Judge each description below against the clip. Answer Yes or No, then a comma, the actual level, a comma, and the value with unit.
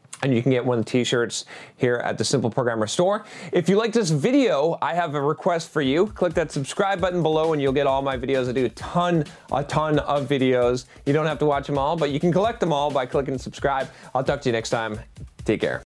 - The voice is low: No, medium, 145 Hz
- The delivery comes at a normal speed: No, fast, 260 wpm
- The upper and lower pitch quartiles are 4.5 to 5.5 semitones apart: Yes, average, 5.2 semitones